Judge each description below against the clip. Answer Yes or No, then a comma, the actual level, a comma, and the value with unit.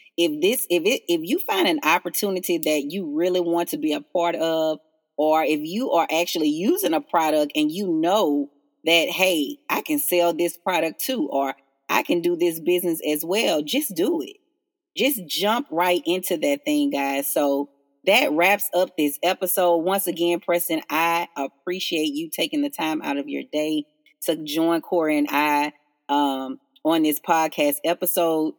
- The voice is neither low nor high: Yes, medium, 170 Hz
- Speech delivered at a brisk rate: No, average, 175 wpm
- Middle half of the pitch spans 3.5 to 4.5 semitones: No, average, 5.0 semitones